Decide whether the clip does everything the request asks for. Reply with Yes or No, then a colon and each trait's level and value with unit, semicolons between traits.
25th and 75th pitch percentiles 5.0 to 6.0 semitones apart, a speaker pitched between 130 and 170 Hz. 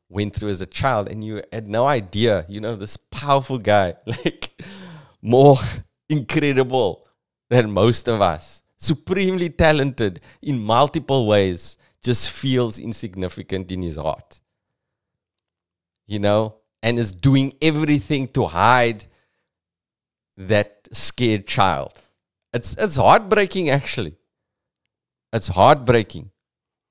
No: average, 5.3 semitones; low, 115 Hz